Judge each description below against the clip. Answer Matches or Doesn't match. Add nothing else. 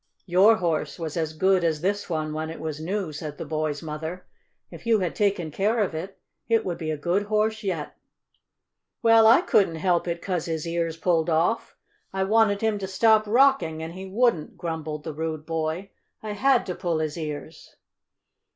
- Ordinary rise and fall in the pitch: Matches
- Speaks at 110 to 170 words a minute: Doesn't match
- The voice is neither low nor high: Matches